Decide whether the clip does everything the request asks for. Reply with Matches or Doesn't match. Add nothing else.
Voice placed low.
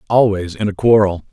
Matches